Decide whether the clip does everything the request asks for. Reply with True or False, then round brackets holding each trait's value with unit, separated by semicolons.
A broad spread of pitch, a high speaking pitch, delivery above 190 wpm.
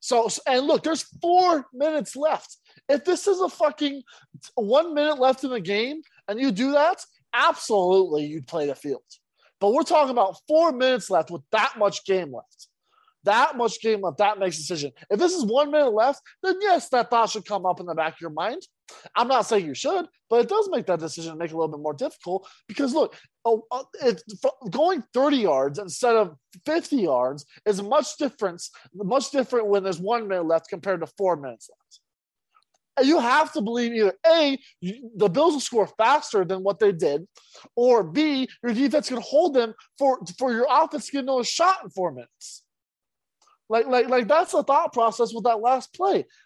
True (7.4 semitones; 240 Hz; 205 wpm)